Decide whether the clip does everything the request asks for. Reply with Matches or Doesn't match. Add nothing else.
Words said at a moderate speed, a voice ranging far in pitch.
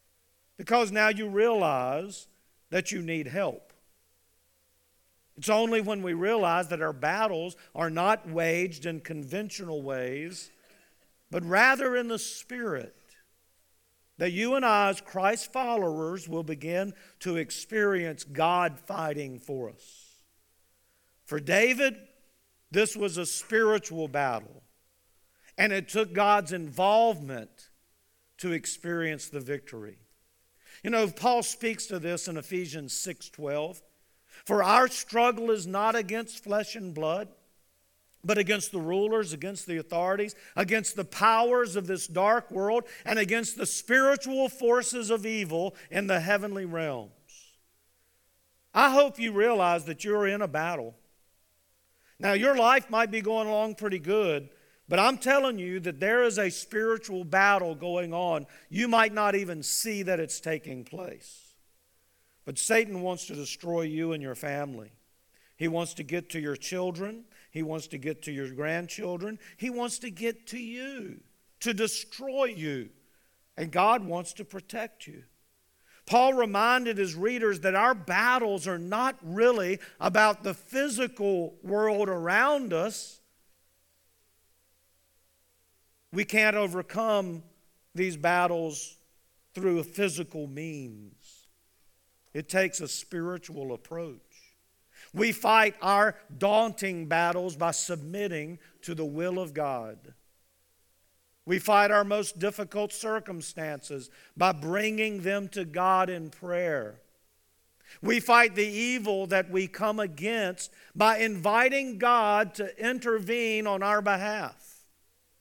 Doesn't match